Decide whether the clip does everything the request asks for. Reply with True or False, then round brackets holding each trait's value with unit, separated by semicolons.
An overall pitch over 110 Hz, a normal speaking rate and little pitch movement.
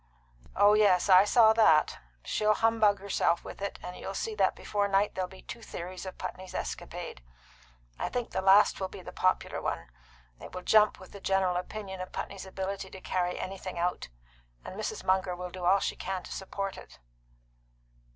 True (190 Hz; 190 wpm; 1.7 semitones)